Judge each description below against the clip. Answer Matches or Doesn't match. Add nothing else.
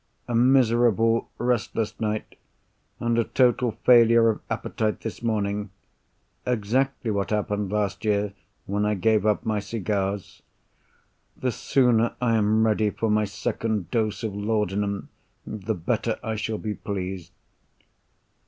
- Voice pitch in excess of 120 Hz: Doesn't match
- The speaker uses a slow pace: Matches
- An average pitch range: Doesn't match